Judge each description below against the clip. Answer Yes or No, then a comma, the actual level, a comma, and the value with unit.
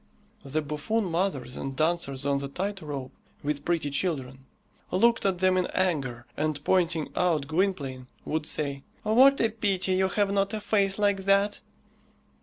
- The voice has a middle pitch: Yes, medium, 175 Hz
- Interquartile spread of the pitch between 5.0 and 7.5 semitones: Yes, wide, 5.5 semitones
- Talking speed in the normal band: Yes, average, 160 wpm